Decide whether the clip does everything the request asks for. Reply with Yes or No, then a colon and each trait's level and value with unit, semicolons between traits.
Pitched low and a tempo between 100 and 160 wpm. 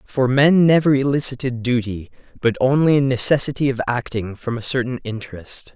Yes: low, 130 Hz; average, 155 wpm